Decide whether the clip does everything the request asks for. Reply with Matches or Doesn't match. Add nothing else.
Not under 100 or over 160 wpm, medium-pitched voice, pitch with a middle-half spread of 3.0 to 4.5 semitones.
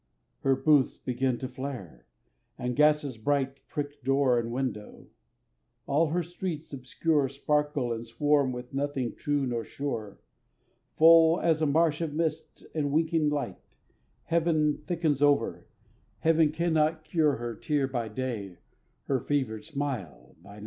Matches